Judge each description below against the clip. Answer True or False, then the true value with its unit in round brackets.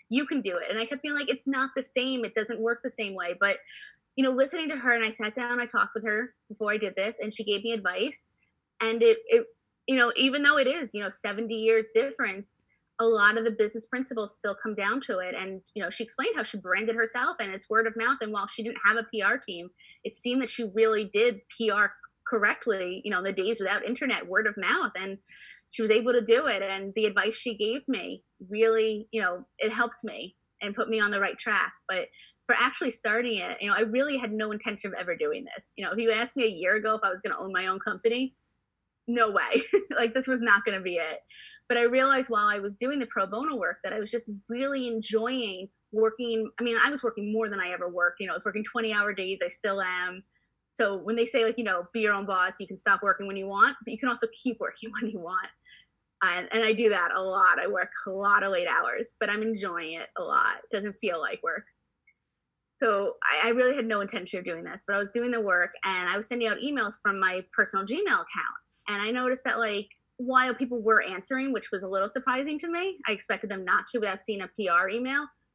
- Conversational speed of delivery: False (255 wpm)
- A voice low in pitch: False (225 Hz)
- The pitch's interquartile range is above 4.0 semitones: False (3.4 semitones)